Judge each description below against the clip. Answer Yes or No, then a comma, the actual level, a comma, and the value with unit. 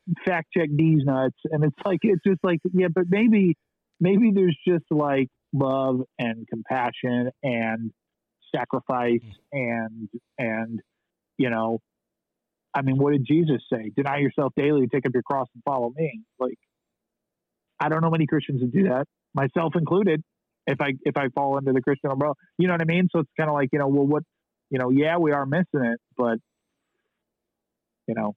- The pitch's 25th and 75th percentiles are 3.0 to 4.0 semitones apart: No, average, 4.4 semitones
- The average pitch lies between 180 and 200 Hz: No, medium, 140 Hz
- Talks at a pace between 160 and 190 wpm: Yes, average, 180 wpm